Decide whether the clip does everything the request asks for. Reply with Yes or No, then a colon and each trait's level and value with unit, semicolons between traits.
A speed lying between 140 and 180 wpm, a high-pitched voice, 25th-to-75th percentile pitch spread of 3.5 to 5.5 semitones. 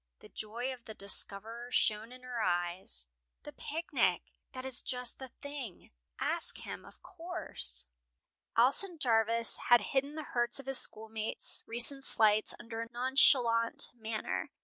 No: average, 145 wpm; high, 235 Hz; average, 3.0 semitones